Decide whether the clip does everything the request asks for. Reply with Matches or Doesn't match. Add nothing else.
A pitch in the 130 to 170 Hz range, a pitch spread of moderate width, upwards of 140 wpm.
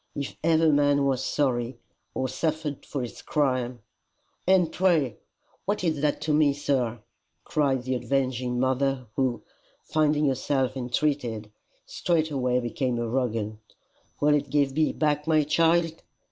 Doesn't match